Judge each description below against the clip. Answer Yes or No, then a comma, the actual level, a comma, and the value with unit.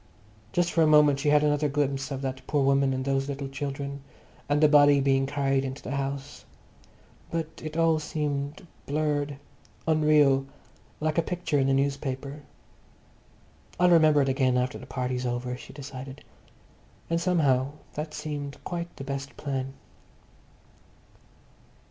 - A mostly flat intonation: Yes, narrow, 1.9 semitones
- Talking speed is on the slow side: No, average, 150 wpm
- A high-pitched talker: No, medium, 140 Hz